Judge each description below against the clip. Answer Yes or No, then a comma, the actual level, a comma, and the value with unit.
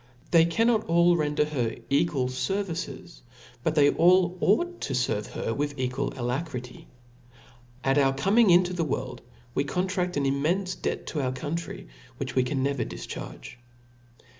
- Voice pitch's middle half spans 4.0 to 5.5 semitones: Yes, average, 4.9 semitones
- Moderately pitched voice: Yes, medium, 150 Hz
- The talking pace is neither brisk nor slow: Yes, average, 150 wpm